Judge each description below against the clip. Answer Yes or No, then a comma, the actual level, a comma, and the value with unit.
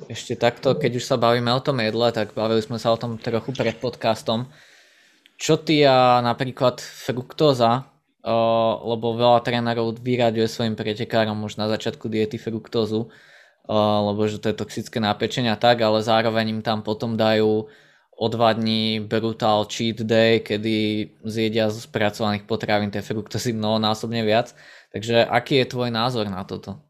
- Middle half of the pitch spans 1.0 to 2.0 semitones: Yes, narrow, 1.6 semitones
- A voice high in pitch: No, low, 115 Hz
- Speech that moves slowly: No, average, 160 wpm